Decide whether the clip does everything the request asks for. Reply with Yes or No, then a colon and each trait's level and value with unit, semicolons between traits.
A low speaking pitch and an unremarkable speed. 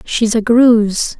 No: high, 225 Hz; average, 150 wpm